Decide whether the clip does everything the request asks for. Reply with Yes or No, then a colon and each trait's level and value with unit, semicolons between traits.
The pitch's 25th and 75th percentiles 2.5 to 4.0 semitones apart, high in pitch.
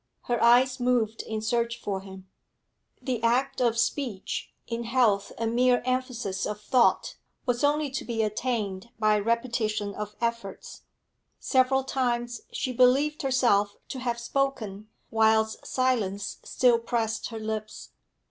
Yes: average, 2.8 semitones; high, 235 Hz